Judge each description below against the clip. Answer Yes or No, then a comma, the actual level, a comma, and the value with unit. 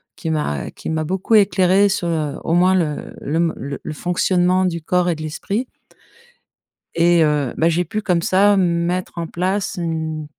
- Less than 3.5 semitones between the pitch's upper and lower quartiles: Yes, narrow, 2.6 semitones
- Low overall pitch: No, medium, 170 Hz